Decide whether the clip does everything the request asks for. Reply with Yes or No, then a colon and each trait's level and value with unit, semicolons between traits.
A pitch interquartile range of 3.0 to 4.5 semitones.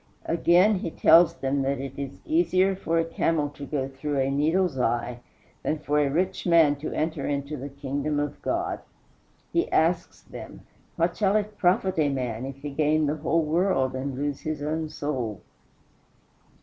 Yes: average, 3.4 semitones